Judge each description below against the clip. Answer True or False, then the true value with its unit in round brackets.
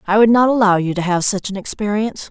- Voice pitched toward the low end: False (205 Hz)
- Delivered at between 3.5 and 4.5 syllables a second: False (6.5 syllables/s)